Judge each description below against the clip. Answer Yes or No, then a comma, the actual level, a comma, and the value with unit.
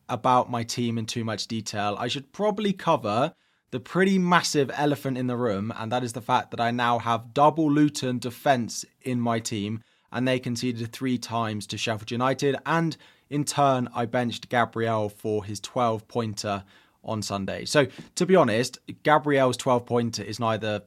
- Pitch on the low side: Yes, low, 120 Hz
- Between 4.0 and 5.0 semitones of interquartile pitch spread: No, average, 3.4 semitones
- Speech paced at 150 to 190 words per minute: Yes, average, 180 wpm